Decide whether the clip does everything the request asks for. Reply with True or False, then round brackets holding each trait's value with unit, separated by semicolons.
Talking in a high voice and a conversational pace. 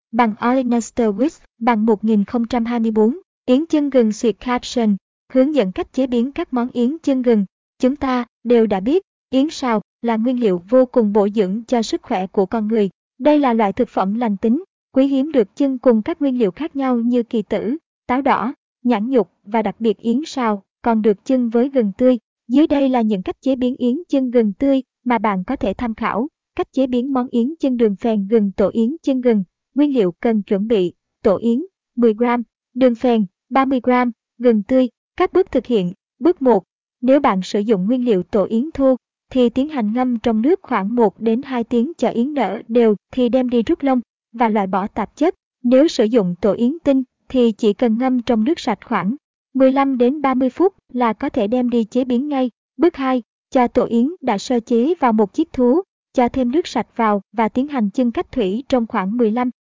True (245 Hz; 210 wpm)